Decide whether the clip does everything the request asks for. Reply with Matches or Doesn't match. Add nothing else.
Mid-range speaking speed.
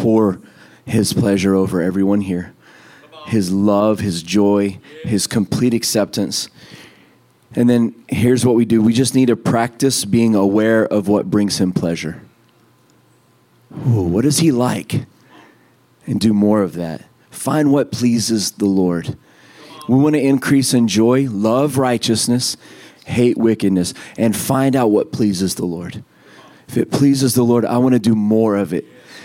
Matches